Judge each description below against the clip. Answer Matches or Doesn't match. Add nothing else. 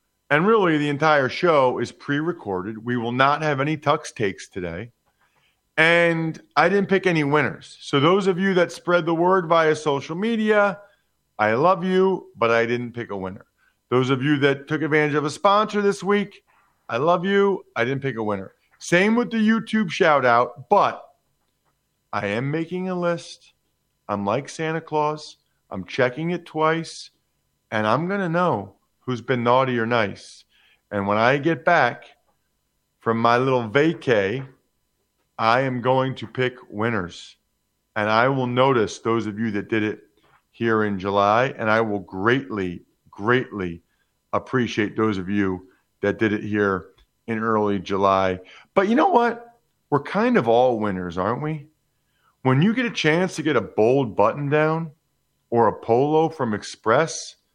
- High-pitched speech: Doesn't match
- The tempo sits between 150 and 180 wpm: Matches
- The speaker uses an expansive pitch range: Matches